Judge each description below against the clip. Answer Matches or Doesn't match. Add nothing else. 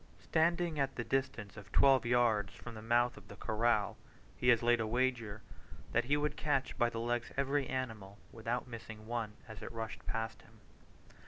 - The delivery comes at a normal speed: Matches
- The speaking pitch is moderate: Doesn't match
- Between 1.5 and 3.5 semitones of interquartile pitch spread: Matches